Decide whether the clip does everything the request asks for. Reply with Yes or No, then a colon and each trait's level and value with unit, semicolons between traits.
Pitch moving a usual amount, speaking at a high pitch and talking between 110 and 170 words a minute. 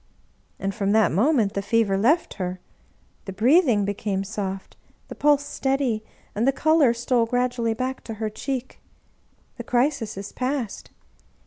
Yes: average, 4.5 semitones; high, 230 Hz; average, 155 wpm